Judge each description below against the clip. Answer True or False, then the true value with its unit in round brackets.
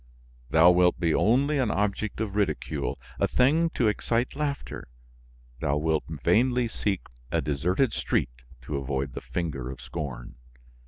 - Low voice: True (90 Hz)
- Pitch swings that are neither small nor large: False (8.4 semitones)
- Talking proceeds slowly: False (145 wpm)